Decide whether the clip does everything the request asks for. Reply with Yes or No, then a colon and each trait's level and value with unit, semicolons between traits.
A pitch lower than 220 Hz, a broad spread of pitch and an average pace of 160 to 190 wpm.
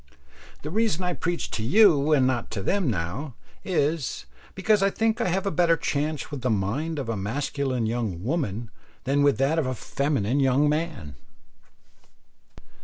Yes: medium, 140 Hz; wide, 5.8 semitones; average, 170 wpm